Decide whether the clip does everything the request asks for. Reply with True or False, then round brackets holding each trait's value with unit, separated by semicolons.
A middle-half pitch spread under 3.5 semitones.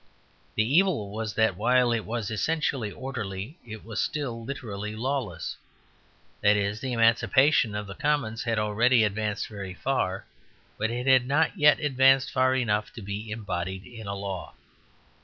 False (4.0 semitones)